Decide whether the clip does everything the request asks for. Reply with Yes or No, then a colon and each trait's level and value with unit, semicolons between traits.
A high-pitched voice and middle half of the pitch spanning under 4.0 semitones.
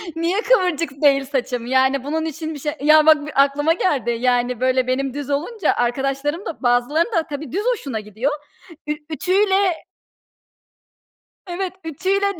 No: very high, 290 Hz; average, 4.4 semitones